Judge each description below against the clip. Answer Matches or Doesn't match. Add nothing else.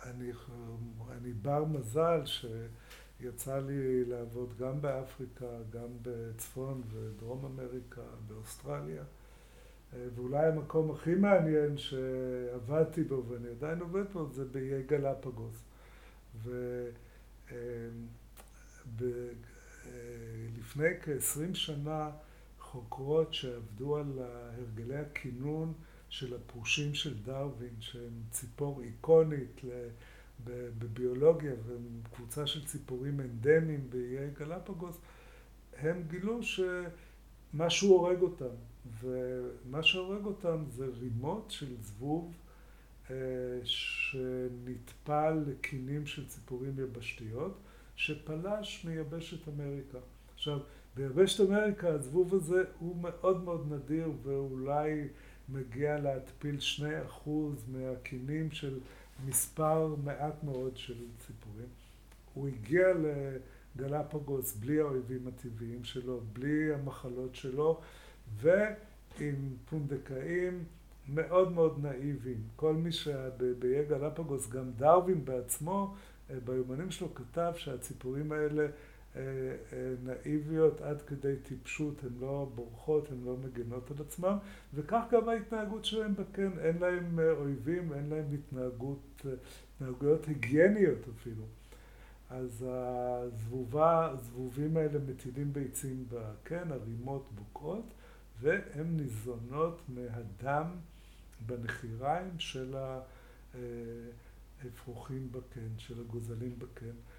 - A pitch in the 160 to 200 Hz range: Doesn't match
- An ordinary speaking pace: Doesn't match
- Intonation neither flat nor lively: Matches